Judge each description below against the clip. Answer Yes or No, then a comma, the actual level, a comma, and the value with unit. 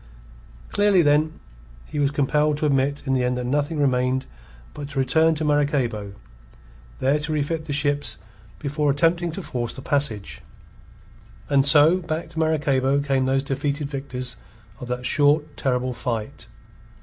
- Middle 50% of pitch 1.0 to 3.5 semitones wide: Yes, narrow, 2.5 semitones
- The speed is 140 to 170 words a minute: Yes, average, 150 wpm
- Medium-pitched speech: Yes, medium, 145 Hz